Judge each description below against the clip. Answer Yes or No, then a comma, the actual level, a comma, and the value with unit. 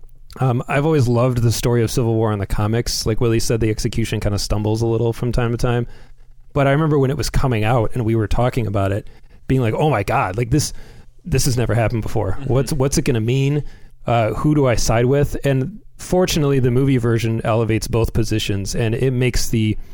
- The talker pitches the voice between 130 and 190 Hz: No, low, 120 Hz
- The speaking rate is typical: No, fast, 230 wpm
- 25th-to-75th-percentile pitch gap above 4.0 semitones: No, average, 3.1 semitones